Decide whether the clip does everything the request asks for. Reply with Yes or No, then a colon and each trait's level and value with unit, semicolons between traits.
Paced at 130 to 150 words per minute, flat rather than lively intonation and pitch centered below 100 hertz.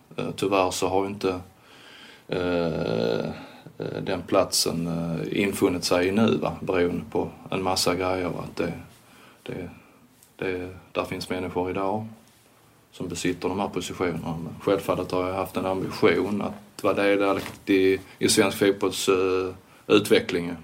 Yes: average, 140 wpm; narrow, 1.8 semitones; very low, 90 Hz